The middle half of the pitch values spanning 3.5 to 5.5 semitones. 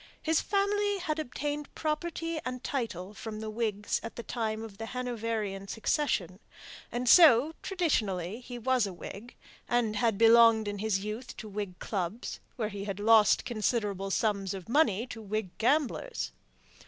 Yes: average, 3.9 semitones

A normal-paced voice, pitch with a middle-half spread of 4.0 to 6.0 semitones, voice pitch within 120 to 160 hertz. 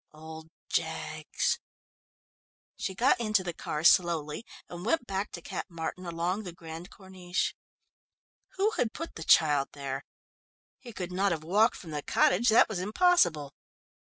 No: average, 150 wpm; average, 4.6 semitones; medium, 175 Hz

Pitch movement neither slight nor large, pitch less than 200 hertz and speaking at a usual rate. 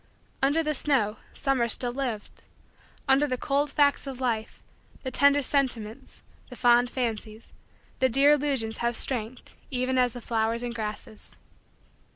No: average, 3.2 semitones; very high, 250 Hz; average, 145 wpm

